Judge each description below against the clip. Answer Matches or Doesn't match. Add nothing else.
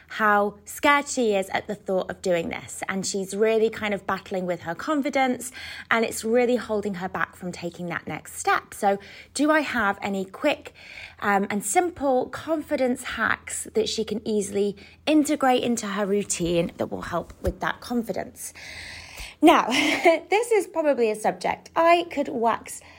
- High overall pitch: Matches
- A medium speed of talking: Matches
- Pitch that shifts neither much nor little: Doesn't match